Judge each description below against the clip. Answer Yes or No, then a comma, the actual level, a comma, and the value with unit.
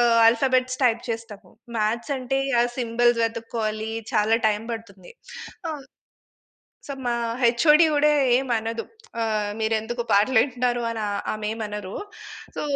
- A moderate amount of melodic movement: No, narrow, 2.2 semitones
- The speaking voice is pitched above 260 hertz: No, high, 230 Hz